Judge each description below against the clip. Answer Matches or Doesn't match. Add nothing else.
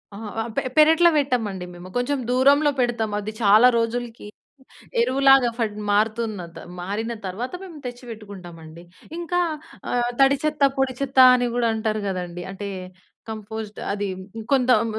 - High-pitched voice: Matches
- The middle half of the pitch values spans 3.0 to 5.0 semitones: Matches